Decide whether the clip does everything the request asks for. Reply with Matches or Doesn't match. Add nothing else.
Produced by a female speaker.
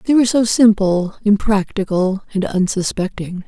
Matches